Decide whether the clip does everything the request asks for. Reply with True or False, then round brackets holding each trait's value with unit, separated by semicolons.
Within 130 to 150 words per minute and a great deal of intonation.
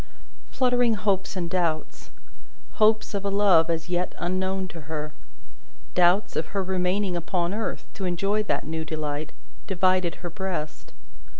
False (140 wpm; 2.9 semitones)